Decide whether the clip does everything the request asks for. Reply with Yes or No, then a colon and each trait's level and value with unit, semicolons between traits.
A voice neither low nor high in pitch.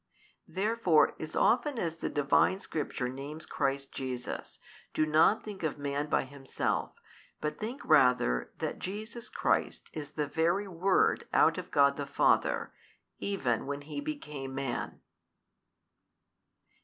Yes: medium, 150 Hz